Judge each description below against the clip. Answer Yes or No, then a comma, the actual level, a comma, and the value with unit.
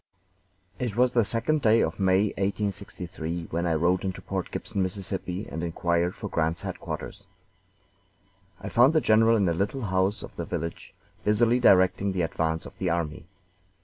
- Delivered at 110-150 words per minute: No, average, 165 wpm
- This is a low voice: Yes, very low, 95 Hz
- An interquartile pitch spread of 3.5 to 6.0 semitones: Yes, average, 4.0 semitones